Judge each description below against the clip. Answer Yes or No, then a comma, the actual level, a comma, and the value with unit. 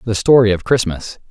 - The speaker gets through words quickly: No, average, 185 wpm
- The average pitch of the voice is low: Yes, low, 110 Hz